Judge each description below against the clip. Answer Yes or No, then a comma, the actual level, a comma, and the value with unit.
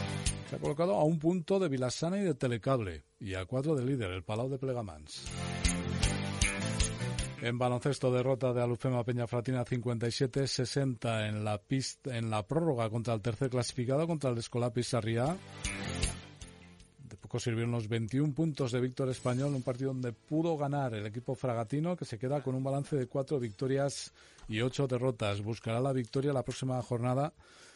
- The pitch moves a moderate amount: Yes, average, 3.3 semitones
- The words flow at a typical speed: Yes, average, 165 wpm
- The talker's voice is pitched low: Yes, low, 125 Hz